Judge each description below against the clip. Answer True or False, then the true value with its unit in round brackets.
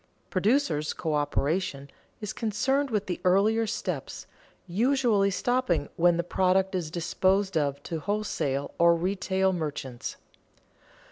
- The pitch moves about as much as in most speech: True (4.6 semitones)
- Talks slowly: True (115 wpm)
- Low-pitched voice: False (185 Hz)